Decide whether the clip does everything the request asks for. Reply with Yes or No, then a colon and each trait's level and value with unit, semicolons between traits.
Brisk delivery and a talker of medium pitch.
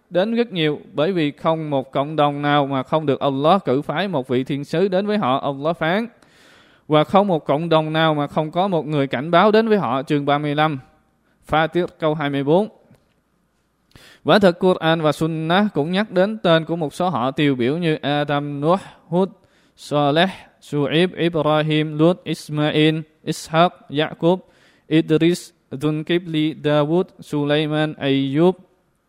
No: slow, 165 wpm; medium, 155 Hz